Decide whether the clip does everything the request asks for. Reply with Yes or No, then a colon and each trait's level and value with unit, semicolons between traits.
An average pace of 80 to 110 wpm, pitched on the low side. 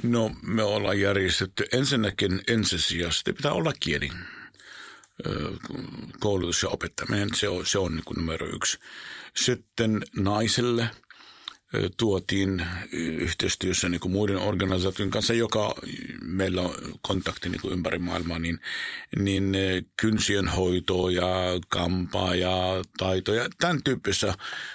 Yes: average, 105 wpm; very low, 95 Hz